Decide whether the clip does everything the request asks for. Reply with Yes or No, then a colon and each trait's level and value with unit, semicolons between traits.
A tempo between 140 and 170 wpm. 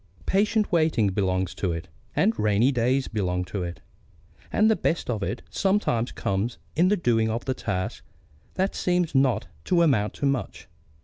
Yes: average, 165 wpm